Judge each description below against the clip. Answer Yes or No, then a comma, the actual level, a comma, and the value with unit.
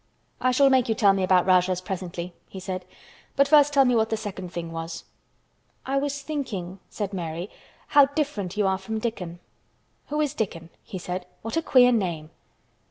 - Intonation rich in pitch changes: Yes, wide, 6.4 semitones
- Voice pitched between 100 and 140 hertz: No, high, 200 Hz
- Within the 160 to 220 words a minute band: Yes, average, 185 wpm